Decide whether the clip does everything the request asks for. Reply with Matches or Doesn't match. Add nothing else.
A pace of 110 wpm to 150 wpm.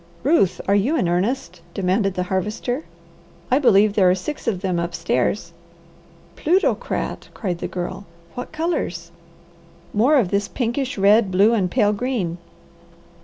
Matches